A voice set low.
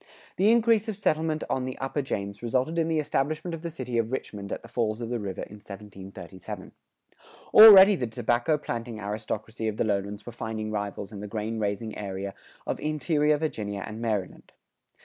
Yes: low, 115 Hz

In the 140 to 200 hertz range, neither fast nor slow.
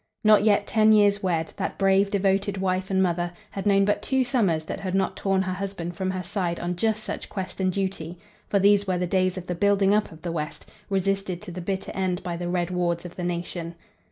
No: high, 190 Hz; fast, 235 wpm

